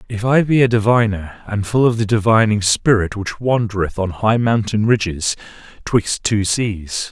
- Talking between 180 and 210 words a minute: No, average, 170 wpm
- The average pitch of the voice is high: No, low, 110 Hz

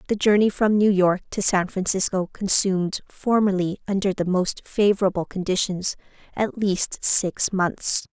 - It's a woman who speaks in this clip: Yes, female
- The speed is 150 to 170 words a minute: No, average, 140 wpm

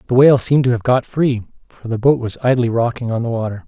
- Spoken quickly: Yes, fast, 260 wpm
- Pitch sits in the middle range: No, low, 120 Hz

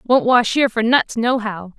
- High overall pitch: Yes, high, 230 Hz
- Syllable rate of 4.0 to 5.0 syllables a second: Yes, 4.6 syllables/s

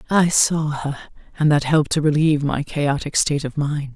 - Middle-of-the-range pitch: Yes, medium, 150 Hz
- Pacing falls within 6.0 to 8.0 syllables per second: No, 5.4 syllables/s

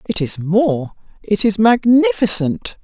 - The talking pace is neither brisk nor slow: No, slow, 105 wpm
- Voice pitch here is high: Yes, high, 200 Hz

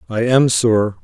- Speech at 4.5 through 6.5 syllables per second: No, 3.8 syllables/s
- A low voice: Yes, low, 115 Hz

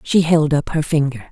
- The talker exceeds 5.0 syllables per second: Yes, 5.4 syllables/s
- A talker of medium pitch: Yes, medium, 150 Hz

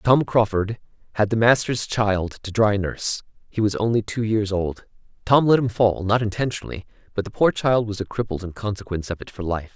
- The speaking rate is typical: No, fast, 210 wpm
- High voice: No, low, 105 Hz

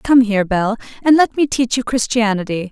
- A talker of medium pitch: No, high, 230 Hz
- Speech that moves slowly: No, average, 200 wpm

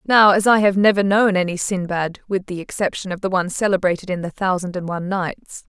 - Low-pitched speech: No, high, 190 Hz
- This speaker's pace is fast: Yes, fast, 220 wpm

